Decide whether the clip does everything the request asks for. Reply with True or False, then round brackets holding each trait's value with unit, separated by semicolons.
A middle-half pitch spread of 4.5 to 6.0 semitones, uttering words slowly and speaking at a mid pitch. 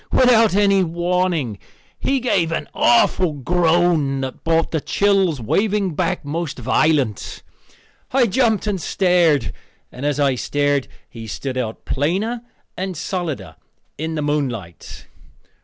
True (5.4 semitones; 125 wpm; 165 Hz)